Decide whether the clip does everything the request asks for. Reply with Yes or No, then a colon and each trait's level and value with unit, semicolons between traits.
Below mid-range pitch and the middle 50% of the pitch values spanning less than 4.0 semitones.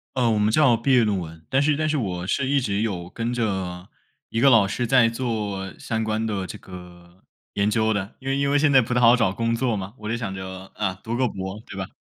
No: low, 110 Hz; average, 4.3 semitones